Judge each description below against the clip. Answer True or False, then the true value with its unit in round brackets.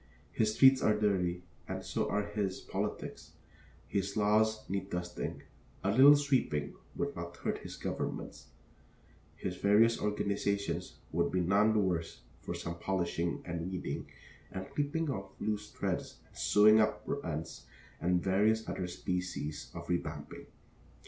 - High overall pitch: False (100 Hz)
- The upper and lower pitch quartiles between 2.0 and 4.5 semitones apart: True (3.5 semitones)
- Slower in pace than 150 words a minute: True (140 wpm)